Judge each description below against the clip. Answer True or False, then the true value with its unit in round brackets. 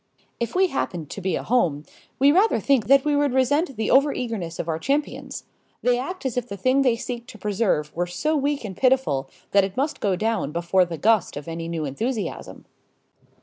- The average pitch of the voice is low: False (230 Hz)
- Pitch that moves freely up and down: True (7.4 semitones)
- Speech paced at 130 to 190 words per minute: False (205 wpm)